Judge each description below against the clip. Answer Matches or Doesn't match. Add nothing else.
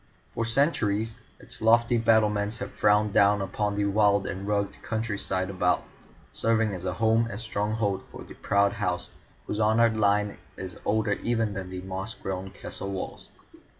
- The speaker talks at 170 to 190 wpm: Doesn't match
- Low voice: Matches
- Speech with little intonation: Matches